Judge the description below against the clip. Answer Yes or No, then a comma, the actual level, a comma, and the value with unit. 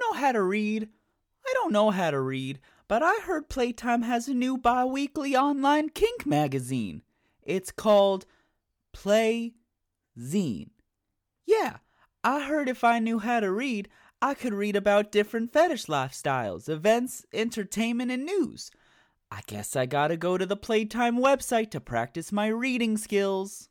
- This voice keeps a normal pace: Yes, average, 150 wpm